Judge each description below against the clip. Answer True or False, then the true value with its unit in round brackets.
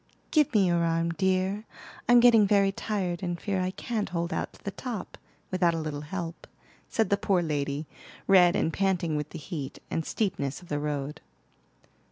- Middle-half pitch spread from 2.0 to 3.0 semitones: False (3.5 semitones)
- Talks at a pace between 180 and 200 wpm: True (185 wpm)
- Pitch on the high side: False (180 Hz)